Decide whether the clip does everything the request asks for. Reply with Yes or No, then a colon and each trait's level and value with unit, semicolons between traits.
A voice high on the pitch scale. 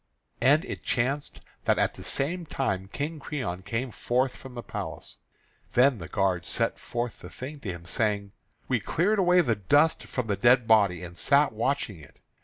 No: low, 120 Hz